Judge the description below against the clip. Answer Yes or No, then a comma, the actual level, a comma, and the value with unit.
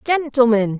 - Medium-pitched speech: No, very high, 250 Hz